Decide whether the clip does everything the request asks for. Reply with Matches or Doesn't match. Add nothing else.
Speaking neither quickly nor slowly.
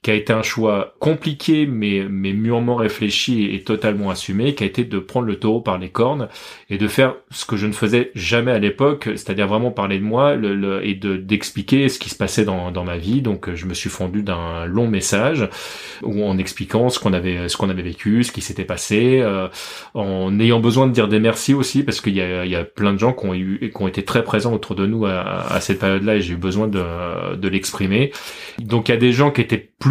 Doesn't match